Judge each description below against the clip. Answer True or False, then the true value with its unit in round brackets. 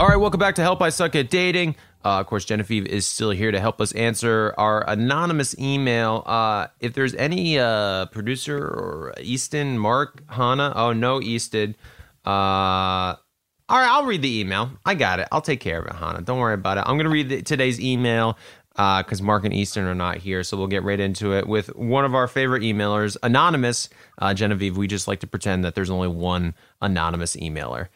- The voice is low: True (110 Hz)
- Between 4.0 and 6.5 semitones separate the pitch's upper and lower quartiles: True (5.0 semitones)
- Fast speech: True (210 wpm)